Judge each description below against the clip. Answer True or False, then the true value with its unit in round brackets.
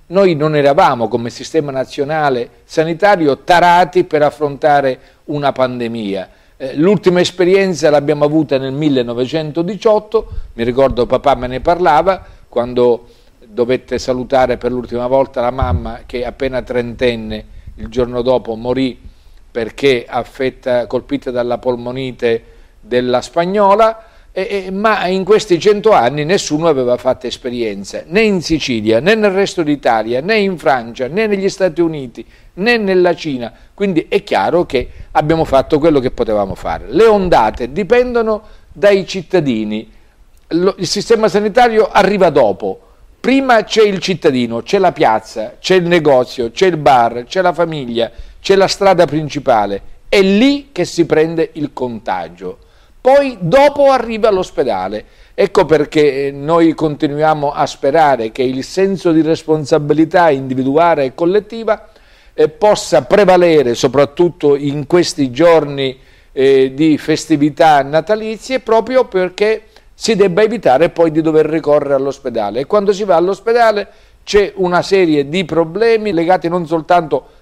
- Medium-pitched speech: True (155 Hz)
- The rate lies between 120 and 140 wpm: True (135 wpm)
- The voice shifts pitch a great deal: True (7.2 semitones)